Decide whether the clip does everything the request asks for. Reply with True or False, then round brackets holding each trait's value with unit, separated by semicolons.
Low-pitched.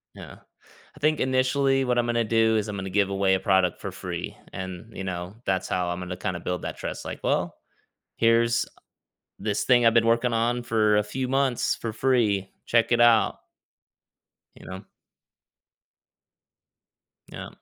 True (115 Hz)